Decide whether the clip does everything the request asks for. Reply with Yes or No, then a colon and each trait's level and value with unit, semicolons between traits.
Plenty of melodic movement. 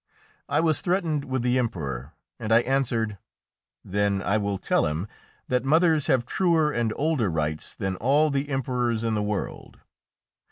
Yes: wide, 6.0 semitones